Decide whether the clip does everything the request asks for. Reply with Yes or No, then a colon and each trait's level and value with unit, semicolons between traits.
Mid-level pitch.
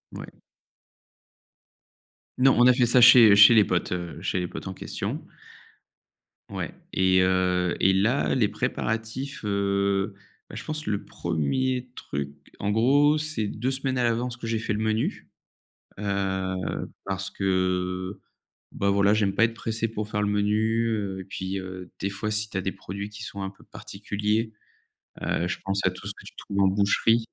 No: low, 100 Hz